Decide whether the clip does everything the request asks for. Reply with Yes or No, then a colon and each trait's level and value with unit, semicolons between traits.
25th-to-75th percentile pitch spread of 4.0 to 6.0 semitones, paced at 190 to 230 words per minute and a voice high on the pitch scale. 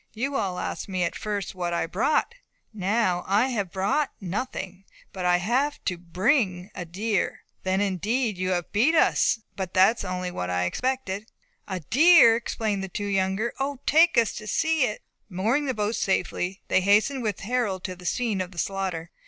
Yes: average, 4.4 semitones; average, 195 wpm; high, 200 Hz